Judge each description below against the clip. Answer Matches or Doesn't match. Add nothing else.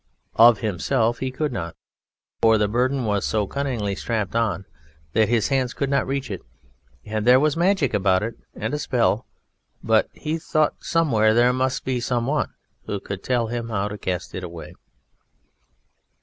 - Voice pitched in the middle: Doesn't match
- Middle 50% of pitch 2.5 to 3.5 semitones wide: Doesn't match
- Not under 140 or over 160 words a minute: Doesn't match